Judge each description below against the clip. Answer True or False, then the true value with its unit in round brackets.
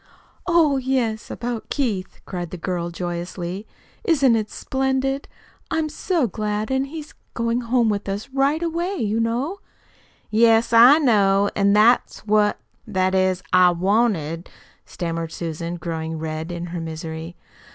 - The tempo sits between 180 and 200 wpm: False (140 wpm)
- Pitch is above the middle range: True (210 Hz)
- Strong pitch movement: True (6.9 semitones)